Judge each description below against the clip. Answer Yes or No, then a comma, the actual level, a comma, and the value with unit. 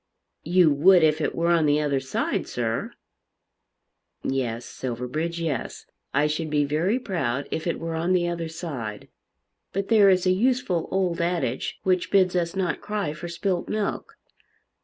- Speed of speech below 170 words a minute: Yes, average, 160 wpm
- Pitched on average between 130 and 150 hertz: No, medium, 170 Hz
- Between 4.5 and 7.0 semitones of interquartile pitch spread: No, average, 3.7 semitones